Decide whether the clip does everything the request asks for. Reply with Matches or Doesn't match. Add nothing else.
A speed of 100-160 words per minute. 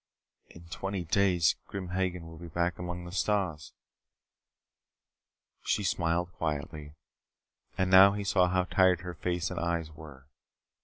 Matches